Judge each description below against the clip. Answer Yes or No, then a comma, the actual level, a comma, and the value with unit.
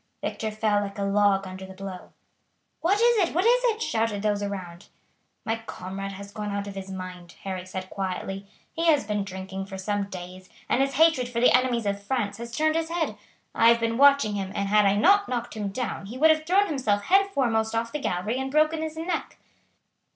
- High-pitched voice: Yes, high, 215 Hz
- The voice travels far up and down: Yes, wide, 6.4 semitones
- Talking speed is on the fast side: Yes, fast, 215 wpm